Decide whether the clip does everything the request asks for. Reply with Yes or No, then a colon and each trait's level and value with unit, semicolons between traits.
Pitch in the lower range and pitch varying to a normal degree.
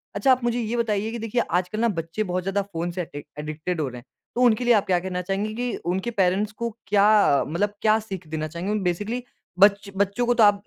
No: high, 200 Hz; average, 3.8 semitones